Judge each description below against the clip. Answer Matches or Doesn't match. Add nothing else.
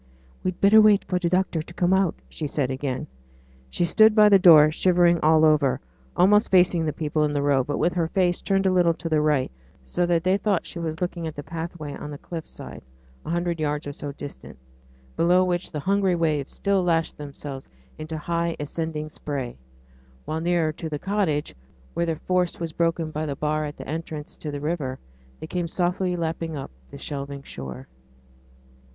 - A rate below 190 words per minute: Doesn't match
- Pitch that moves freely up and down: Doesn't match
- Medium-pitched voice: Matches